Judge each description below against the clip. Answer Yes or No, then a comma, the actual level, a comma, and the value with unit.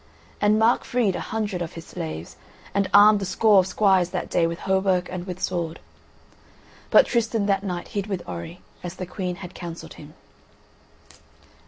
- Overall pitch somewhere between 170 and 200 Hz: Yes, medium, 185 Hz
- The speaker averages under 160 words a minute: No, average, 175 wpm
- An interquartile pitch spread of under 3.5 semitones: Yes, average, 2.8 semitones